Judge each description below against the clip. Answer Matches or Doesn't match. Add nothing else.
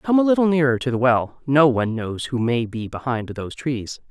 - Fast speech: Matches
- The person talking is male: Doesn't match